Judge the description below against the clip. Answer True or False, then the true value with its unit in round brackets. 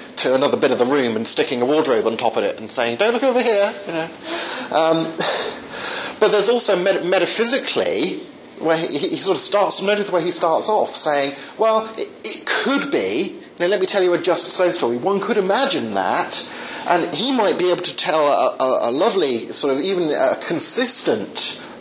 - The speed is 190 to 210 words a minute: True (205 wpm)